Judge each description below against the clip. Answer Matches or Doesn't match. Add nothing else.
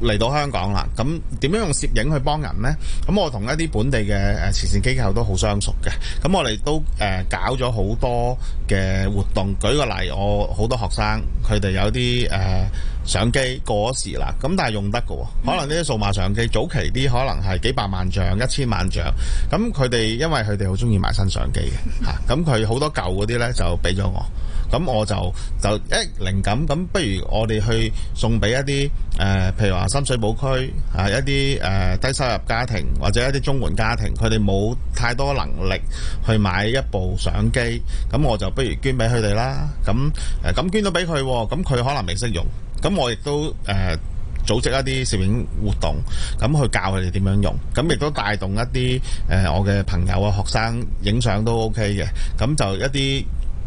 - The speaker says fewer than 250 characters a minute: Doesn't match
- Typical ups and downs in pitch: Matches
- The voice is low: Matches